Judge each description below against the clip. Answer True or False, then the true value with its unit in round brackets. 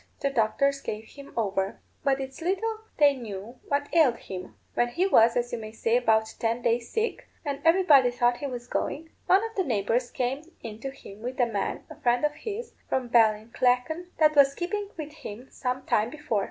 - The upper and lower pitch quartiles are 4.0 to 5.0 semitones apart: True (4.6 semitones)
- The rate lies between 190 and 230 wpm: True (200 wpm)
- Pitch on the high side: True (250 Hz)